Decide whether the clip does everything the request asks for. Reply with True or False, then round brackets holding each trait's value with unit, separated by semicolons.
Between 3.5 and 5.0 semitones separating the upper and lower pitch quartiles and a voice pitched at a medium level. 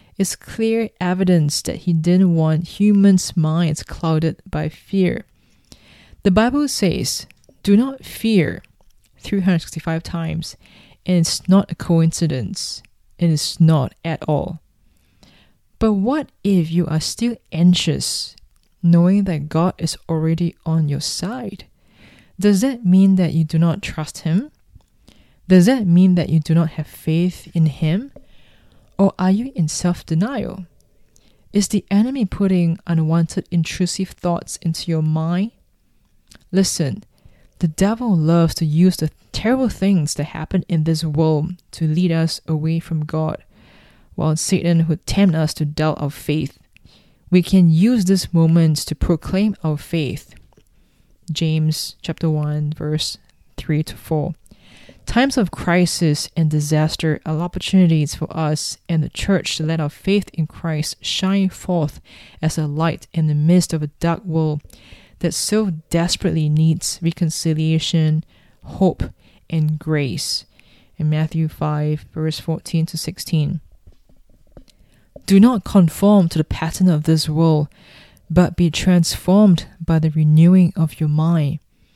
False (2.8 semitones; 165 Hz)